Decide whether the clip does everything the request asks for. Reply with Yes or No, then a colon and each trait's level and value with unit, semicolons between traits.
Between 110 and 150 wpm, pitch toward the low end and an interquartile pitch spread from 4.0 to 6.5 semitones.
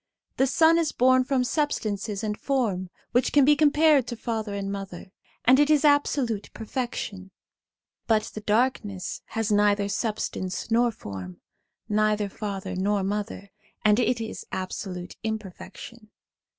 No: slow, 135 wpm; high, 215 Hz; average, 4.3 semitones